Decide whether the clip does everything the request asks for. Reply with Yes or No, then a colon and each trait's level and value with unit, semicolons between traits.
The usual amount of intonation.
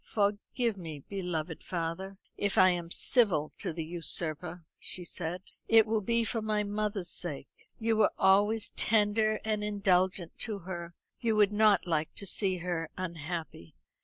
Yes: average, 3.7 semitones